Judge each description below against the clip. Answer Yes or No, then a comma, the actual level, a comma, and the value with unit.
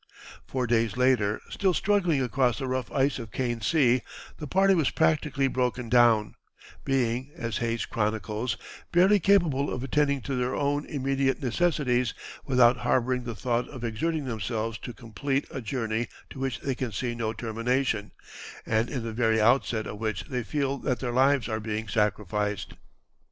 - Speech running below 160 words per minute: No, average, 165 wpm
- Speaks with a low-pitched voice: Yes, low, 125 Hz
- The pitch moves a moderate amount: Yes, average, 3.3 semitones